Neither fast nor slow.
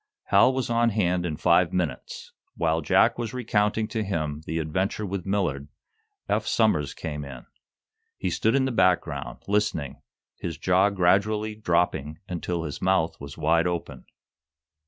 Yes: average, 150 wpm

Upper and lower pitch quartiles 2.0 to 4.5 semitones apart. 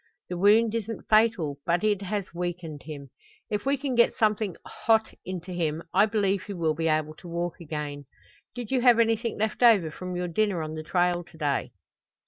No: average, 5.0 semitones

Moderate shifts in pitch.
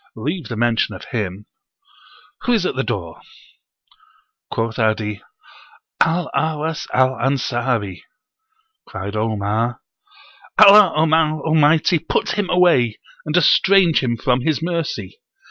No: wide, 6.3 semitones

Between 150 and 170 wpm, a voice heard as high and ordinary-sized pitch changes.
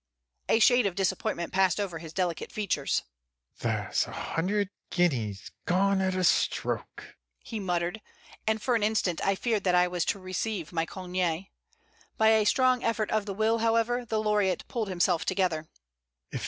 Yes: average, 165 wpm; high, 195 Hz; average, 3.6 semitones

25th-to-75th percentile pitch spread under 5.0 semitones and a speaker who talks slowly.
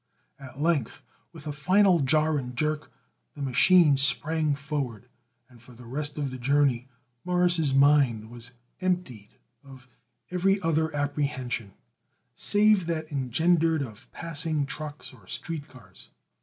Yes: average, 3.9 semitones; slow, 130 wpm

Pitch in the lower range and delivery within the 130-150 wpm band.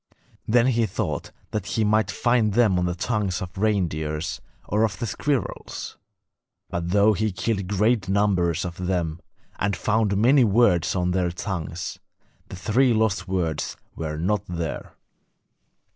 Yes: low, 100 Hz; average, 145 wpm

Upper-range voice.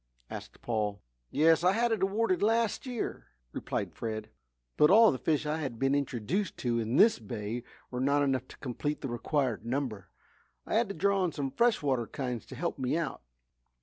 No: medium, 140 Hz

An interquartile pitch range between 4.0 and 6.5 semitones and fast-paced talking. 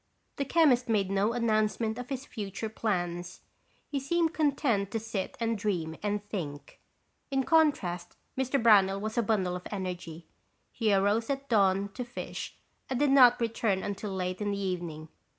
No: average, 4.4 semitones; average, 165 wpm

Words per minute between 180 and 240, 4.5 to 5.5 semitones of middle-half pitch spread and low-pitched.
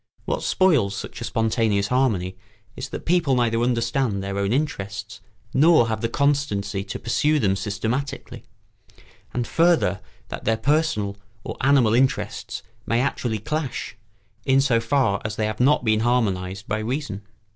No: average, 150 wpm; average, 5.1 semitones; low, 115 Hz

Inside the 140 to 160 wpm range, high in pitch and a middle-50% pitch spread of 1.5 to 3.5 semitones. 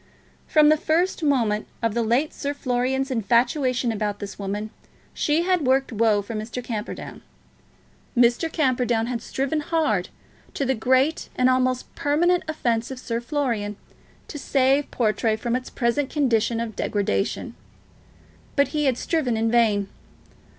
No: average, 145 wpm; very high, 250 Hz; average, 4.1 semitones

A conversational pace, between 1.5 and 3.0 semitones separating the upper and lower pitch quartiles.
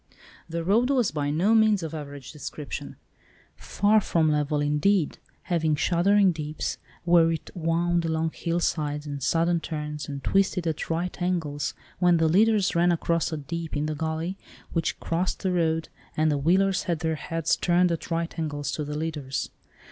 Yes: average, 170 wpm; average, 2.7 semitones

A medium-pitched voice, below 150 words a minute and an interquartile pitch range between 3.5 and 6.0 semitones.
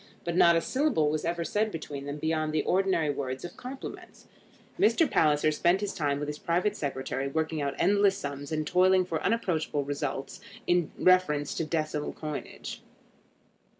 No: medium, 160 Hz; average, 165 wpm; average, 3.8 semitones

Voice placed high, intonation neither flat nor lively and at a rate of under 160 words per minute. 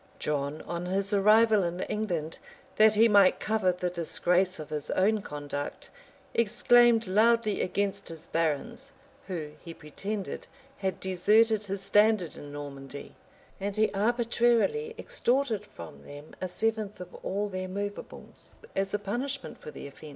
Yes: high, 195 Hz; average, 4.3 semitones; average, 145 wpm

